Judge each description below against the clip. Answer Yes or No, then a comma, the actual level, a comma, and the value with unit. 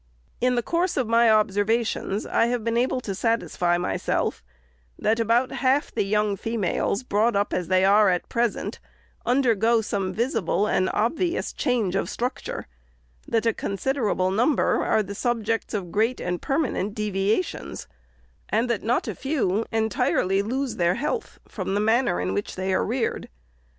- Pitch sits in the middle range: No, high, 220 Hz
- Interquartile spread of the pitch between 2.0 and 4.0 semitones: Yes, average, 3.5 semitones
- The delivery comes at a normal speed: Yes, average, 165 wpm